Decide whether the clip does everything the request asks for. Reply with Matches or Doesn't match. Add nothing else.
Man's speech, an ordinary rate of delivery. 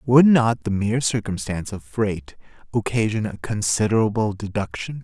Doesn't match